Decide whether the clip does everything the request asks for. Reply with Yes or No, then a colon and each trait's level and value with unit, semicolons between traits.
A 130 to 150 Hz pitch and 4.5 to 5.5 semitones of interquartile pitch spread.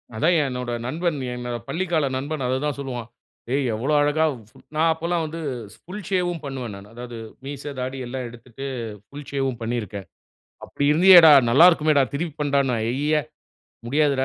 No: medium, 140 Hz; average, 4.1 semitones